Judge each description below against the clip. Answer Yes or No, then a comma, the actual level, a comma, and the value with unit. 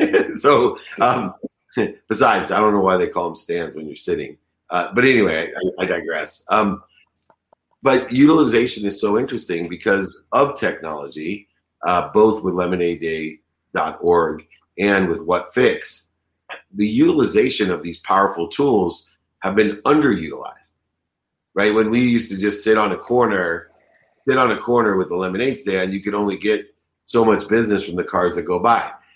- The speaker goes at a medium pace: Yes, average, 155 wpm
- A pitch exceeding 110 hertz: No, low, 100 Hz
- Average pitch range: Yes, average, 3.5 semitones